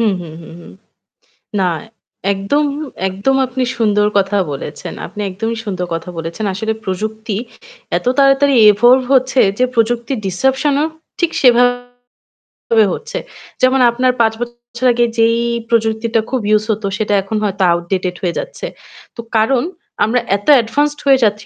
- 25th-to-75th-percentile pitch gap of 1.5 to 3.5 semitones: No, average, 4.0 semitones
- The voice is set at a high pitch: Yes, high, 225 Hz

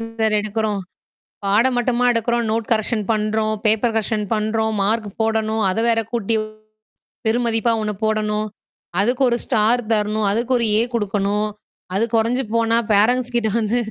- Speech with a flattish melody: Yes, narrow, 1.5 semitones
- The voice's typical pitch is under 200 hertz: No, high, 220 Hz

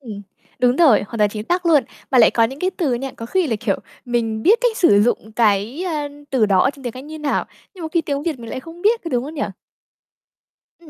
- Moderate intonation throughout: No, wide, 6.3 semitones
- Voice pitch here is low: No, very high, 265 Hz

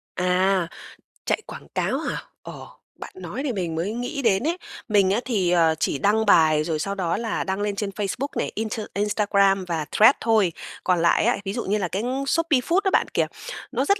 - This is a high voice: Yes, high, 200 Hz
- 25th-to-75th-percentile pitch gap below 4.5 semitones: Yes, average, 3.9 semitones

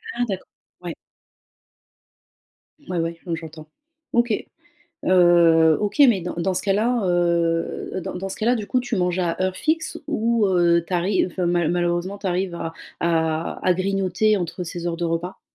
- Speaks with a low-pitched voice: No, medium, 180 Hz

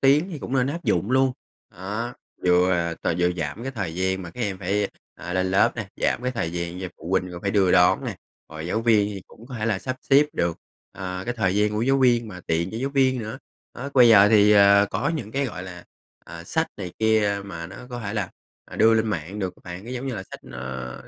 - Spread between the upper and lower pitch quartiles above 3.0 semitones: Yes, average, 4.8 semitones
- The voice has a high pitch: No, low, 100 Hz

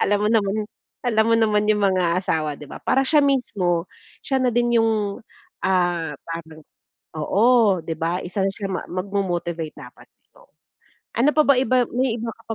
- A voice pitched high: Yes, high, 205 Hz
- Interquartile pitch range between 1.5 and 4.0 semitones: No, average, 5.1 semitones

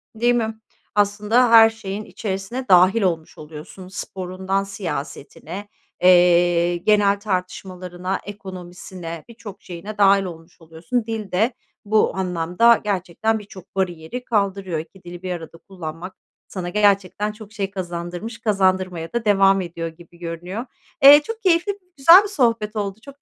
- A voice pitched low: No, high, 195 Hz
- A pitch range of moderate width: Yes, average, 3.4 semitones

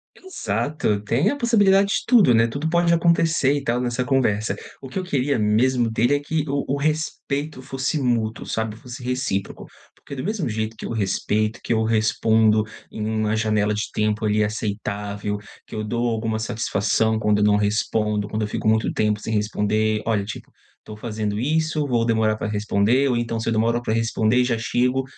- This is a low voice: Yes, low, 115 Hz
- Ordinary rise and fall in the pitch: Yes, average, 3.8 semitones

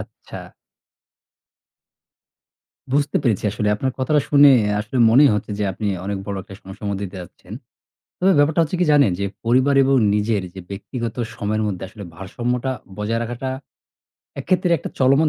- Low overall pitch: Yes, low, 115 Hz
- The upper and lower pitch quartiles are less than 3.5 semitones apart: No, wide, 5.5 semitones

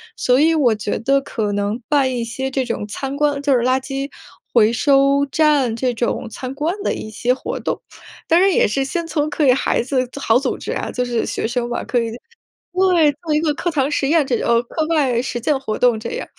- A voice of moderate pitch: No, very high, 265 Hz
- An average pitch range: Yes, average, 3.7 semitones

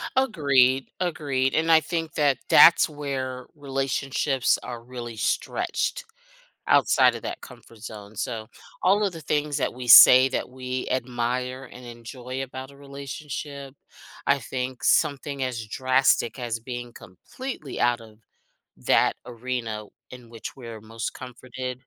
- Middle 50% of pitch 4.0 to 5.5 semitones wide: No, narrow, 2.6 semitones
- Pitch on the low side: Yes, low, 130 Hz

